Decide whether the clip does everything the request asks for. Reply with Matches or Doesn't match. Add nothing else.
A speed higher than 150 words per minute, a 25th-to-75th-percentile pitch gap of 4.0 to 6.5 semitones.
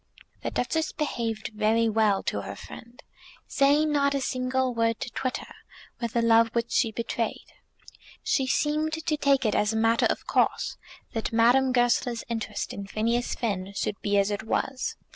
Doesn't match